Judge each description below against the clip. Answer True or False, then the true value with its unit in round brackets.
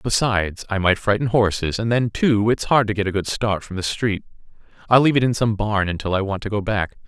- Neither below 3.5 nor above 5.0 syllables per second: False (5.8 syllables/s)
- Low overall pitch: True (105 Hz)